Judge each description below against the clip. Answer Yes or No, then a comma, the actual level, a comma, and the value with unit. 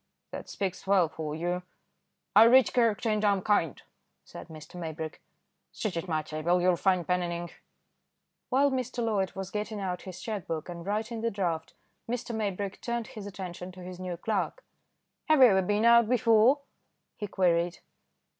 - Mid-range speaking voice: No, high, 195 Hz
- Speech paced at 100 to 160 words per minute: No, average, 175 wpm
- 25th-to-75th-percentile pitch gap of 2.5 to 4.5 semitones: Yes, average, 4.1 semitones